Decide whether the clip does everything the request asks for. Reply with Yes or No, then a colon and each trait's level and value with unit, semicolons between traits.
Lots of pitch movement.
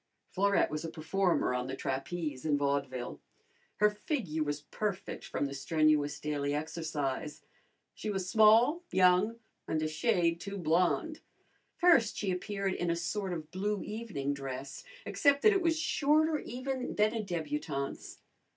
Yes: wide, 6.2 semitones